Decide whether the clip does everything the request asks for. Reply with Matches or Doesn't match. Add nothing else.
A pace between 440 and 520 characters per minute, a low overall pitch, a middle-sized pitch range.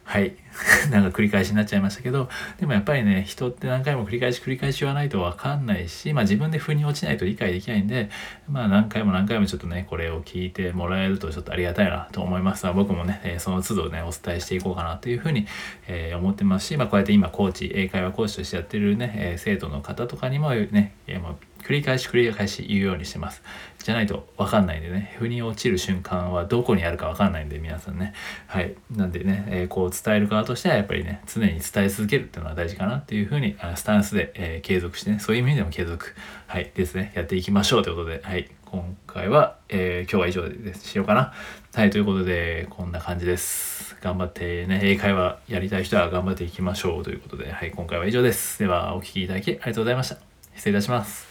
Matches